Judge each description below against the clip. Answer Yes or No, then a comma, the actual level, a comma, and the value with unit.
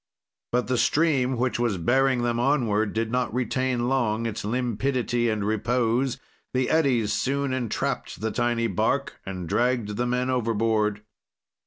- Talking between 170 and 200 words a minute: No, average, 145 wpm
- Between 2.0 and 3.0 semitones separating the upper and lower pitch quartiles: Yes, narrow, 2.6 semitones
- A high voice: No, low, 120 Hz